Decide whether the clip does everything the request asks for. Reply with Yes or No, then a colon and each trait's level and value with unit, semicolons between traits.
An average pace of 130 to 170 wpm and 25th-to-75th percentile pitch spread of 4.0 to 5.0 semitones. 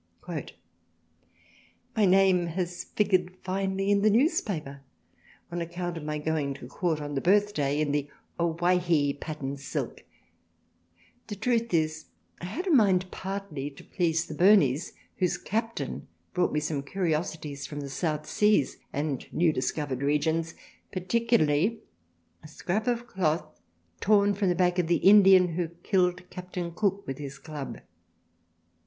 Yes: average, 150 wpm; average, 4.5 semitones